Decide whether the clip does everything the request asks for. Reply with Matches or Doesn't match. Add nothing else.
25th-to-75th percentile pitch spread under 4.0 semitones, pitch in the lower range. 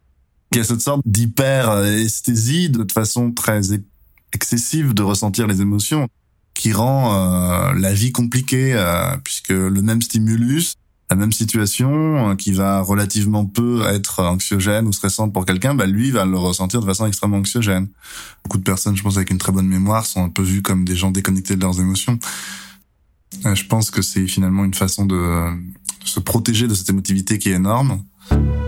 Matches